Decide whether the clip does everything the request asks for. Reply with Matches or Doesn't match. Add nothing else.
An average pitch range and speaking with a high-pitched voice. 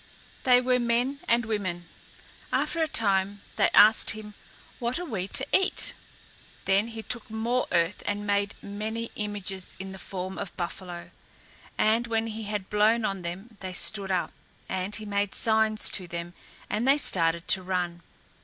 Matches